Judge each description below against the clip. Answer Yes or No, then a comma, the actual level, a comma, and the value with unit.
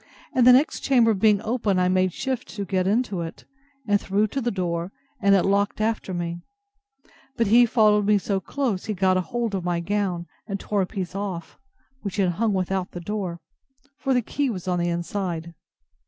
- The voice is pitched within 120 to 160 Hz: No, high, 200 Hz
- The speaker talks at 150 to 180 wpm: No, average, 195 wpm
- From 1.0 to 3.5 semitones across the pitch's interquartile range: Yes, average, 3.2 semitones